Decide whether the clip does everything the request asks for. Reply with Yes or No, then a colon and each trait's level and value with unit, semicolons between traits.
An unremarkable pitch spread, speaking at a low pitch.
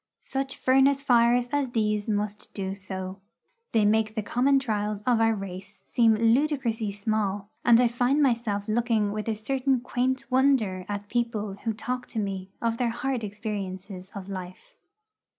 No: average, 3.4 semitones; high, 220 Hz